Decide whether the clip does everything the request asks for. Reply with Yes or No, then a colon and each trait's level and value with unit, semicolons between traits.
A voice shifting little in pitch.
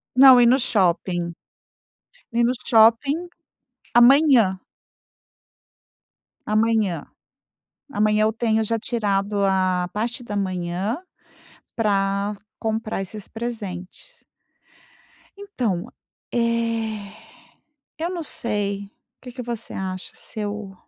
No: average, 3.2 semitones